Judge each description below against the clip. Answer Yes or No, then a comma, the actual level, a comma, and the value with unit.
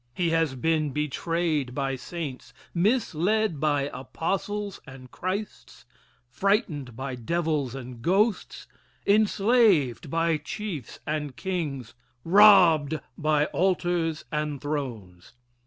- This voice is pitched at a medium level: Yes, medium, 155 Hz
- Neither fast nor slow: No, slow, 100 wpm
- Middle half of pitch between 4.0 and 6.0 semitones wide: Yes, average, 5.1 semitones